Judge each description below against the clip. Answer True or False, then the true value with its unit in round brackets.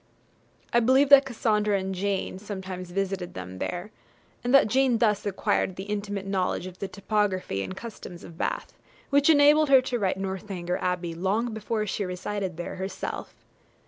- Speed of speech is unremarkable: True (165 wpm)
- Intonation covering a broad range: False (3.4 semitones)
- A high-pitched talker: True (200 Hz)